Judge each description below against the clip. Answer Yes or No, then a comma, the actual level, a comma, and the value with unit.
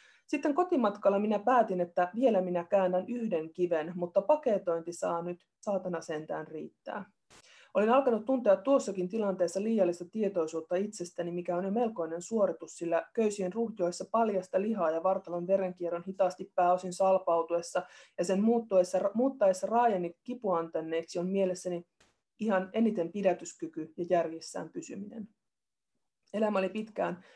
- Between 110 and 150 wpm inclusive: Yes, average, 125 wpm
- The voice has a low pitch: No, high, 190 Hz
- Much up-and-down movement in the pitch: No, average, 4.1 semitones